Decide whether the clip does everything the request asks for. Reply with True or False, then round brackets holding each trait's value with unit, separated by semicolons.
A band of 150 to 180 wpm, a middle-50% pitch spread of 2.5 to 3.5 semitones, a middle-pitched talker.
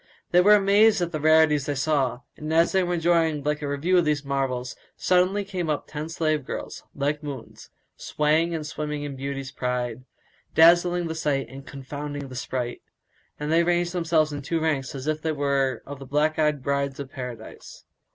False (190 wpm; 3.0 semitones; 150 Hz)